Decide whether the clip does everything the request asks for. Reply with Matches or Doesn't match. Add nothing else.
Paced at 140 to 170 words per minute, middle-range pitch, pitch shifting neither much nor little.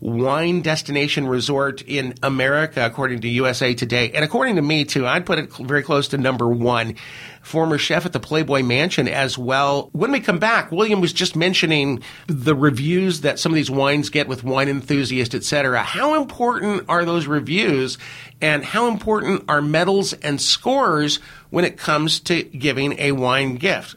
Doesn't match